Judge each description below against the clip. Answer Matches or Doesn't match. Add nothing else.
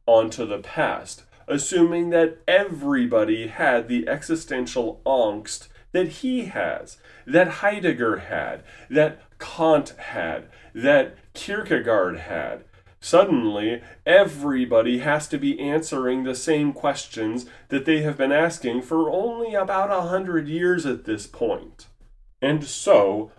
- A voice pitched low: Doesn't match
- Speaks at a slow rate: Matches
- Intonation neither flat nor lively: Doesn't match